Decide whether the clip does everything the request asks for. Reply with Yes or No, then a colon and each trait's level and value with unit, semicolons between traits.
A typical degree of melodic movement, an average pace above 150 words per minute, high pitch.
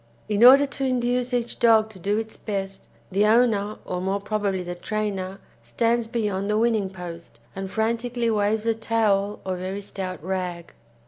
Yes: average, 3.1 semitones; average, 170 wpm; high, 210 Hz